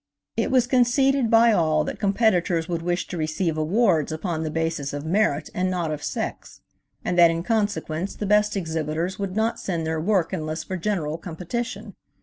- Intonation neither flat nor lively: Yes, average, 4.6 semitones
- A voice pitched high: No, medium, 175 Hz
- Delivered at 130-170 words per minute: No, average, 180 wpm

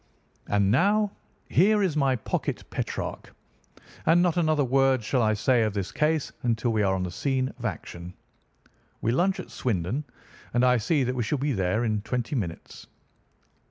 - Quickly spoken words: No, average, 175 wpm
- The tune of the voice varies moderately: No, wide, 5.7 semitones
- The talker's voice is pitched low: Yes, low, 125 Hz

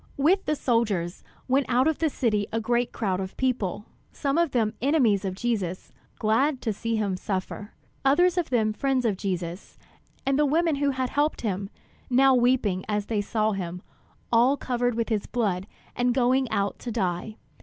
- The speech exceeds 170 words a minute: Yes, average, 180 wpm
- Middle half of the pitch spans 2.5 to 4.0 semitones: No, average, 4.7 semitones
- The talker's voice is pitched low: No, high, 235 Hz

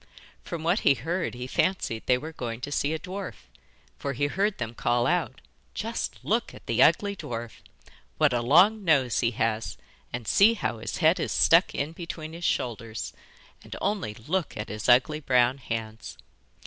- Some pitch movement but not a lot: No, wide, 6.3 semitones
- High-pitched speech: No, low, 135 Hz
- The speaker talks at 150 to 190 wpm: Yes, average, 180 wpm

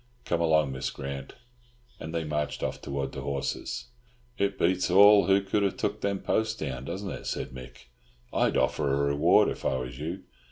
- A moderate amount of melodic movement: No, wide, 5.9 semitones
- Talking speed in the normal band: Yes, average, 190 wpm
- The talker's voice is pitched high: No, very low, 80 Hz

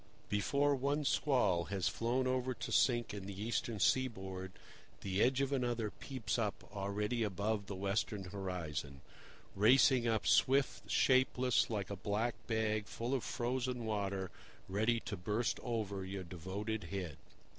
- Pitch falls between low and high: No, low, 110 Hz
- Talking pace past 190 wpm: No, average, 145 wpm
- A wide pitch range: No, average, 4.0 semitones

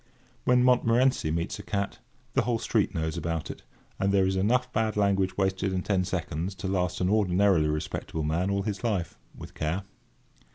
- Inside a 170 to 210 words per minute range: Yes, average, 180 wpm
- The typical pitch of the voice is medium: No, very low, 95 Hz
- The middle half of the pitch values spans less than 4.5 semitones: Yes, average, 3.1 semitones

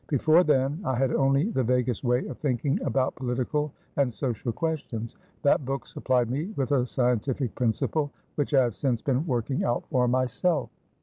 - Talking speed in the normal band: Yes, average, 175 wpm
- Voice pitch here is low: Yes, low, 130 Hz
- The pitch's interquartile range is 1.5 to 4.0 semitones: Yes, average, 2.7 semitones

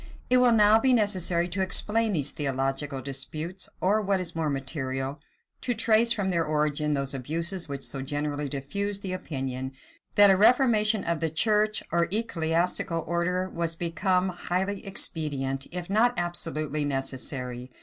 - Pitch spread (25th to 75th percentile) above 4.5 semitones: Yes, wide, 5.6 semitones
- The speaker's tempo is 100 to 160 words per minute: Yes, average, 150 wpm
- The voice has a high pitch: No, medium, 170 Hz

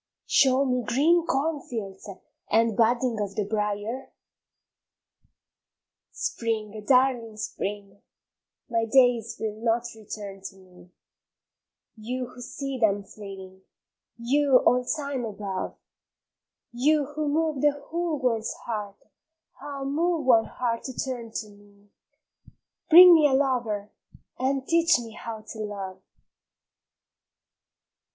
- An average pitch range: Yes, average, 4.5 semitones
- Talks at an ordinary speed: No, slow, 115 wpm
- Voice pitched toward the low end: No, high, 235 Hz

